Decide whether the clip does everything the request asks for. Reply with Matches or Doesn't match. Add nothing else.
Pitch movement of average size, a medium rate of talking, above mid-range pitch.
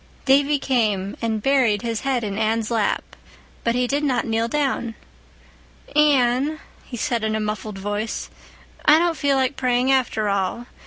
Matches